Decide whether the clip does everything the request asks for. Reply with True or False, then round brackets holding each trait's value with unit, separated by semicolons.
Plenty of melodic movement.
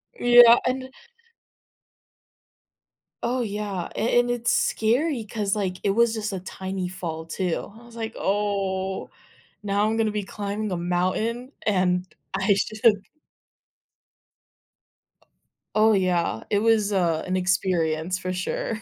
False (3.4 semitones)